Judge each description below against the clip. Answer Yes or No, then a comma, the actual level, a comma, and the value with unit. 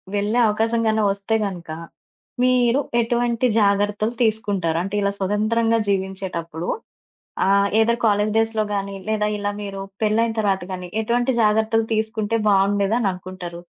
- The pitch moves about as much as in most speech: No, narrow, 2.3 semitones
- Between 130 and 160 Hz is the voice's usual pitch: No, high, 210 Hz